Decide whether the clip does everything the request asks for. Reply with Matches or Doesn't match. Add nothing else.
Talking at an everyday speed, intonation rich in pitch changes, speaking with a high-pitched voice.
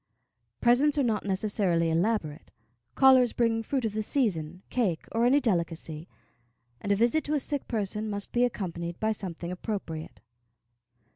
Matches